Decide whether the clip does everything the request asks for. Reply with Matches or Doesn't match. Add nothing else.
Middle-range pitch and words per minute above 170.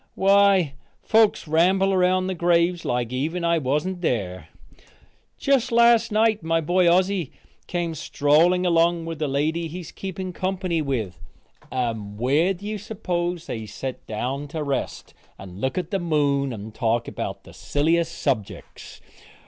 Doesn't match